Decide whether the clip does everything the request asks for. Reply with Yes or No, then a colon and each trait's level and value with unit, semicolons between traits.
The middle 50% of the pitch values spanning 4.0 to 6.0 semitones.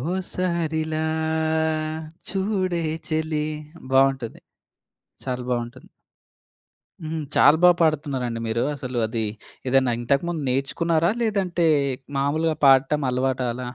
Yes: average, 4.5 semitones